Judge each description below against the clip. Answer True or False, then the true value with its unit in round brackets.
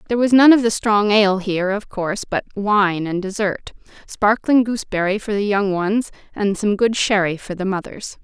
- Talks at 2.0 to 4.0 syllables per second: False (5.2 syllables/s)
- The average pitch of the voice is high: True (205 Hz)